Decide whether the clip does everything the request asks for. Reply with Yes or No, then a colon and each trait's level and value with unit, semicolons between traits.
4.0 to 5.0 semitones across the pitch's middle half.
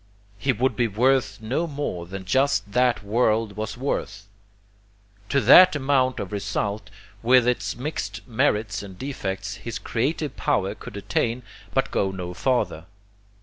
Yes: average, 4.4 semitones